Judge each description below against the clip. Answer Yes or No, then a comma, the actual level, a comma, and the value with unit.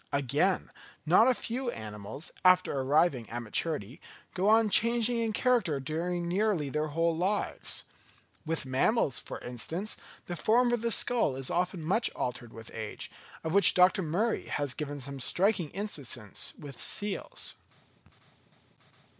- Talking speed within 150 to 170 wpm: No, average, 140 wpm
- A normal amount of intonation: No, wide, 7.3 semitones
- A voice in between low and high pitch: Yes, medium, 170 Hz